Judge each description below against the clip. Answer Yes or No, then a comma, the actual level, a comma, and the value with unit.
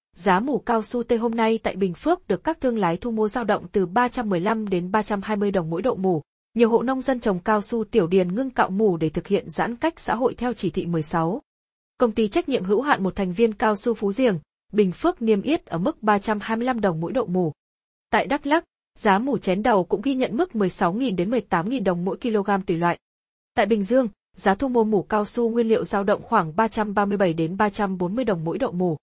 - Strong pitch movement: No, average, 4.1 semitones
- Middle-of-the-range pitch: No, high, 215 Hz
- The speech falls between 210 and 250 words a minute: Yes, average, 235 wpm